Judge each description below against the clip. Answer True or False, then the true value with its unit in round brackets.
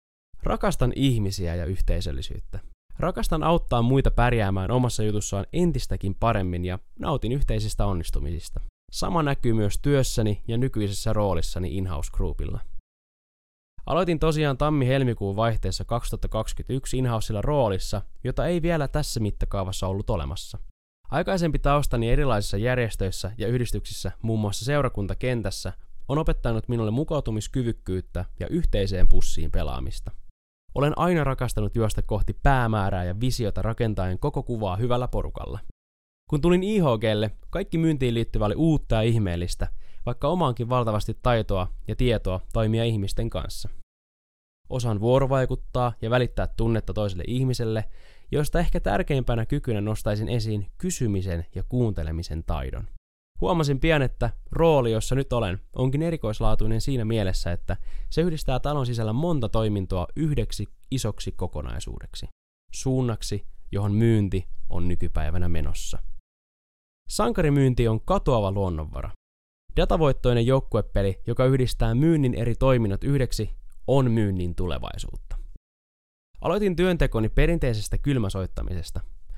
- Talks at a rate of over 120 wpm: False (115 wpm)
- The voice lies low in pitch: True (110 Hz)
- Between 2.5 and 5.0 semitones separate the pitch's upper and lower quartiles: False (5.6 semitones)